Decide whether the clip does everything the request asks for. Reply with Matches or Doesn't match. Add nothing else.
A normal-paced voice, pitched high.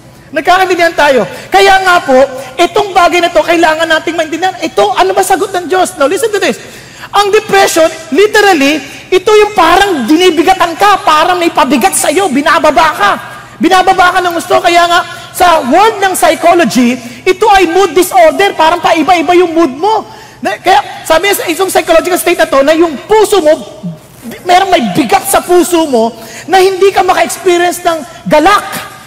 Matches